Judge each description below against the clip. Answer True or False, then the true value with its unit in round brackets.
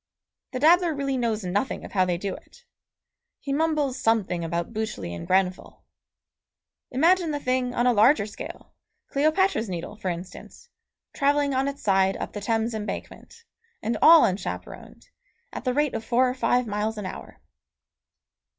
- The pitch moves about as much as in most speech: False (5.8 semitones)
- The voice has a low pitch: False (235 Hz)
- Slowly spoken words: False (160 wpm)